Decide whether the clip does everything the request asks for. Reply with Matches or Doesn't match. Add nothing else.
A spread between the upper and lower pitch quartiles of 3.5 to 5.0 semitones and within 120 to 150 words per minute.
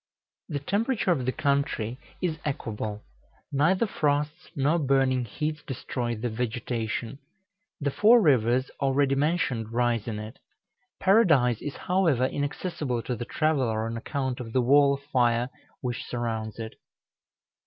Matches